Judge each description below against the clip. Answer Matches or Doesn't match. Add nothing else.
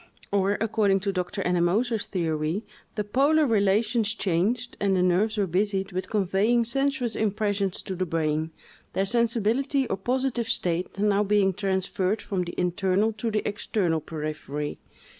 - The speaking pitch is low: Doesn't match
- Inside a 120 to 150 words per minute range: Matches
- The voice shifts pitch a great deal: Doesn't match